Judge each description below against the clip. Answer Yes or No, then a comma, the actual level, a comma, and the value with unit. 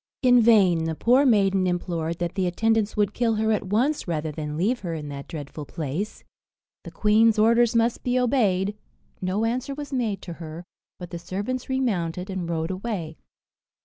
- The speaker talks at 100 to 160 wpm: No, average, 180 wpm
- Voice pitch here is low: No, high, 195 Hz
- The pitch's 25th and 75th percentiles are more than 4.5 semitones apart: Yes, average, 5.3 semitones